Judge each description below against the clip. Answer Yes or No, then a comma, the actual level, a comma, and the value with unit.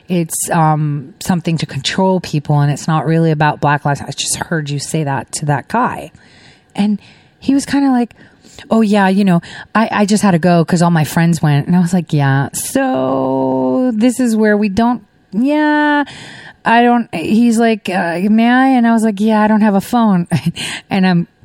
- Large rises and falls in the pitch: Yes, wide, 6.6 semitones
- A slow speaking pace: No, fast, 205 wpm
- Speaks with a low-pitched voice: No, medium, 180 Hz